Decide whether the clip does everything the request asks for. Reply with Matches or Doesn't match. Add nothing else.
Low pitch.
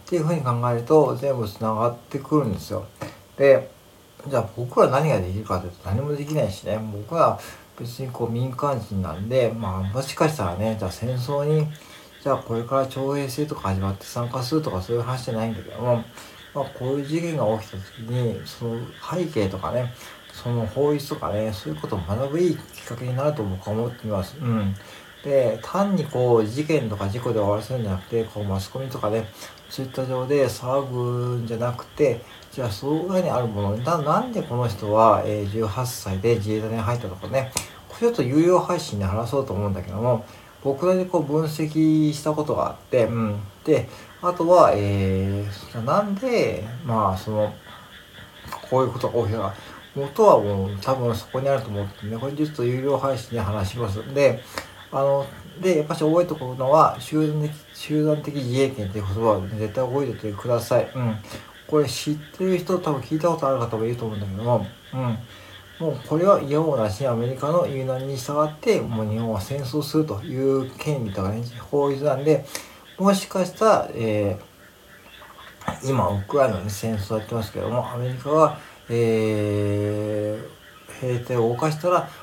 Matches